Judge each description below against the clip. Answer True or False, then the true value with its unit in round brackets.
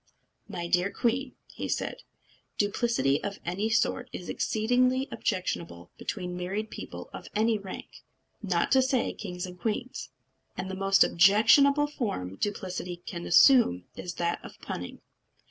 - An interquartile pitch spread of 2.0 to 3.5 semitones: False (4.9 semitones)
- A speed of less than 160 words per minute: True (140 wpm)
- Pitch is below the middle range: False (200 Hz)